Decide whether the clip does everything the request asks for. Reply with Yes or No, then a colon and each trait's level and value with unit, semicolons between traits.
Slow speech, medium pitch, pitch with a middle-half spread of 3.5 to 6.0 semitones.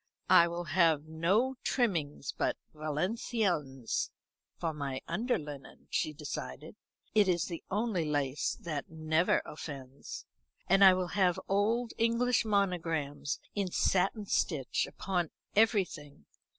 Yes: slow, 120 wpm; medium, 170 Hz; average, 5.0 semitones